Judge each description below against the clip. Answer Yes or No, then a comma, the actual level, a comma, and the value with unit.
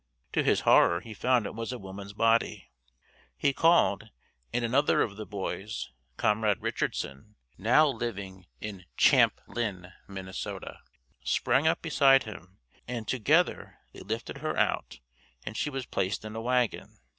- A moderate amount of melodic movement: Yes, average, 4.2 semitones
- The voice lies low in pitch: Yes, low, 110 Hz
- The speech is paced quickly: No, average, 145 wpm